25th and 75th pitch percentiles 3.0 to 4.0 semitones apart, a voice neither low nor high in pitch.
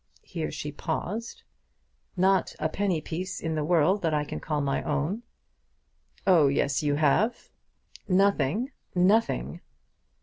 No: average, 4.5 semitones; medium, 165 Hz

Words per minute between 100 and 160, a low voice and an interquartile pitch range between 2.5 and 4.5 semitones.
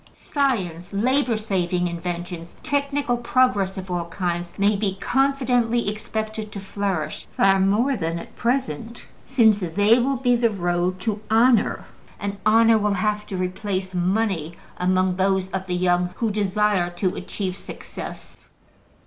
No: average, 140 wpm; high, 200 Hz; average, 4.0 semitones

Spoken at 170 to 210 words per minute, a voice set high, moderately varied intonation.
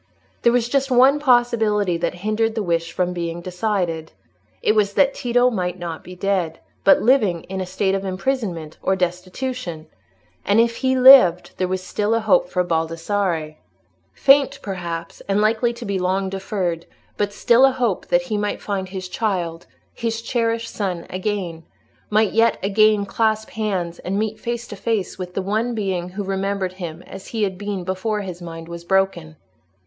Yes: average, 175 wpm; high, 195 Hz; average, 3.9 semitones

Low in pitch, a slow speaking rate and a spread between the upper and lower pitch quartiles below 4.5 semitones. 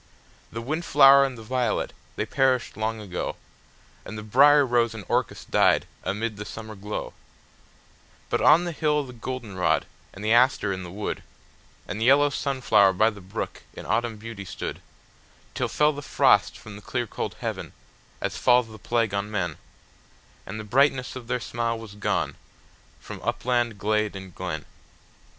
No: low, 115 Hz; average, 160 wpm; average, 3.7 semitones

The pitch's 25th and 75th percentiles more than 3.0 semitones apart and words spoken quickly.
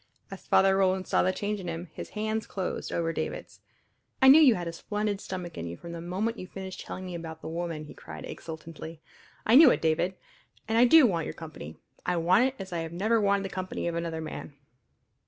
Yes: average, 3.8 semitones; fast, 225 wpm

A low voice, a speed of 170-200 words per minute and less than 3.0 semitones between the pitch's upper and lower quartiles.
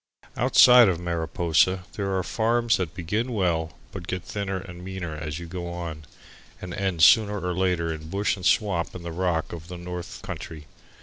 Yes: very low, 90 Hz; average, 185 wpm; narrow, 2.5 semitones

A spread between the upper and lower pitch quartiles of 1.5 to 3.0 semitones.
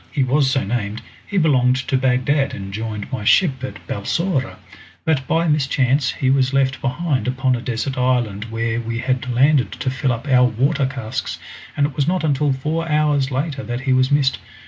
Yes: narrow, 2.4 semitones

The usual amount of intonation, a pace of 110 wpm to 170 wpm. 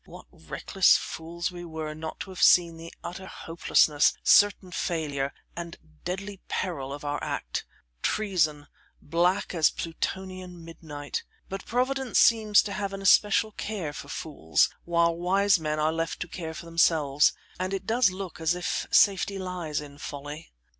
Yes: average, 3.5 semitones; average, 155 wpm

